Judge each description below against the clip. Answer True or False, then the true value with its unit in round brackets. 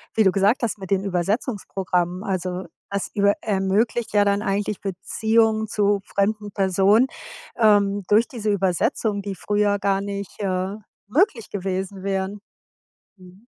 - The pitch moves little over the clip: True (1.7 semitones)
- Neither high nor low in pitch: False (200 Hz)